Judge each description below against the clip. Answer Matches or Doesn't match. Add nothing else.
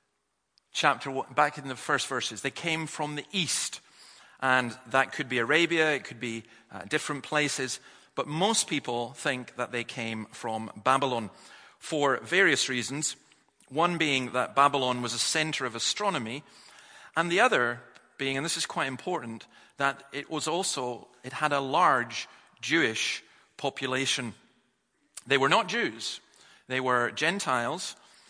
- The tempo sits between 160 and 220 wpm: Doesn't match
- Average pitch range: Matches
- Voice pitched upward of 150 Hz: Doesn't match